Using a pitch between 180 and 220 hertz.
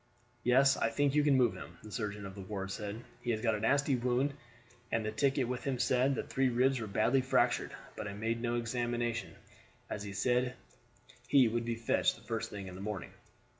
No: low, 120 Hz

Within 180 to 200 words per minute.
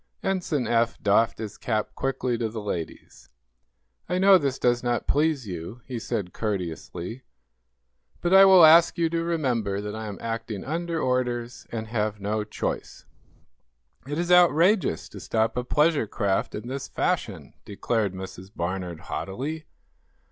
No: average, 150 wpm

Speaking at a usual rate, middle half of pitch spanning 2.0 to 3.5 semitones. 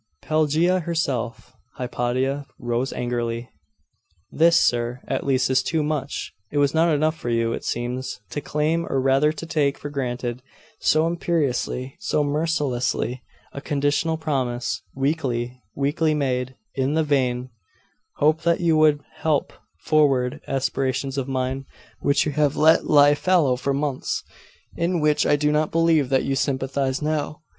Yes: average, 150 wpm; average, 3.2 semitones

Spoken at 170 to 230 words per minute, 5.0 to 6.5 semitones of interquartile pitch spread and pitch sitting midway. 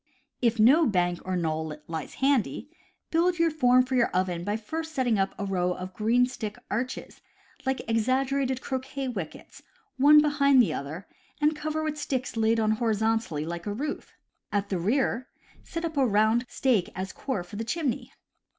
No: average, 175 wpm; wide, 5.6 semitones; high, 235 Hz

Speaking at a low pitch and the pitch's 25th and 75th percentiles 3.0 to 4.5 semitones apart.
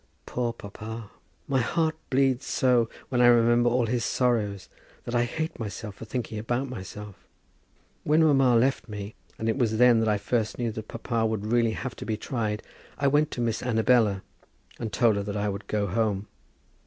No: low, 115 Hz; narrow, 2.6 semitones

